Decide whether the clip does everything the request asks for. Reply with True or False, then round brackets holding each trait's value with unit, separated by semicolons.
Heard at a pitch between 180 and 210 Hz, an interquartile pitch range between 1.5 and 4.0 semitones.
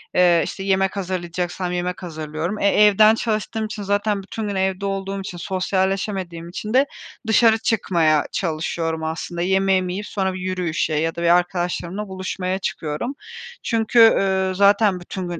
True (190 Hz; 2.5 semitones)